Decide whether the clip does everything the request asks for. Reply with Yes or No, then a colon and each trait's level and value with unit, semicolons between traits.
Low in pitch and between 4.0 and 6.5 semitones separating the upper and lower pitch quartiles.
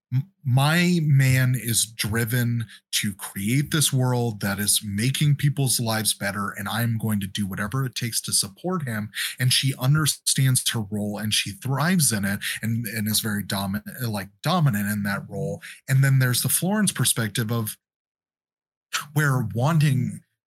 Yes: low, 120 Hz; average, 4.4 semitones